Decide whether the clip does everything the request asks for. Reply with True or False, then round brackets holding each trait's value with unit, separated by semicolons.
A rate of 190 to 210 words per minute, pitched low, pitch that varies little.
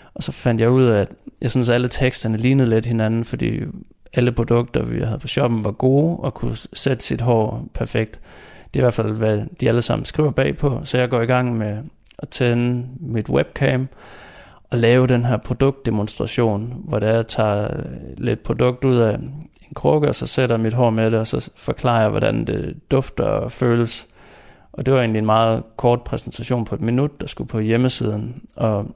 True (205 wpm; 120 Hz; 2.3 semitones)